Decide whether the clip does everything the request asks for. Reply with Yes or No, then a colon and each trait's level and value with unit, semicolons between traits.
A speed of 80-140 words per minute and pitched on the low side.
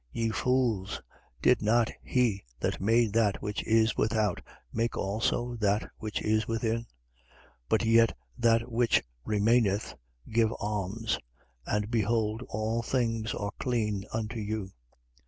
Yes: slow, 135 wpm; low, 110 Hz